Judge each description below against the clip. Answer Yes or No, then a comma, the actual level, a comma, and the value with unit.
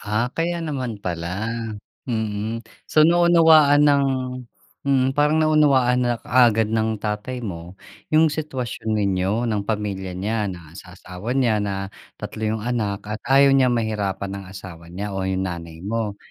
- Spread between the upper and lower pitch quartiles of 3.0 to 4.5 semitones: No, average, 4.9 semitones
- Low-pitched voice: Yes, low, 110 Hz